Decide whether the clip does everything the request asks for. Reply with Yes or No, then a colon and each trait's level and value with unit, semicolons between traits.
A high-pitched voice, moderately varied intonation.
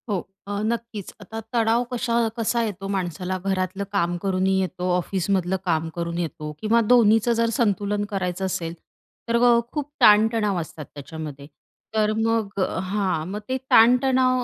Yes: high, 200 Hz; average, 4.0 semitones